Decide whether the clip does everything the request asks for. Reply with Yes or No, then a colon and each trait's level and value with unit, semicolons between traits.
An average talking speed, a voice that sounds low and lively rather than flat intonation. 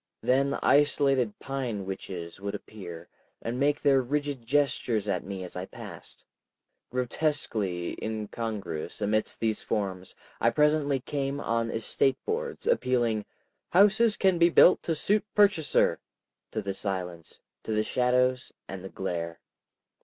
No: slow, 130 wpm; low, 120 Hz; wide, 6.4 semitones